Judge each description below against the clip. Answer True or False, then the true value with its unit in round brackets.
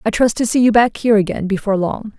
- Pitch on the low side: False (215 Hz)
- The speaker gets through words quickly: True (275 wpm)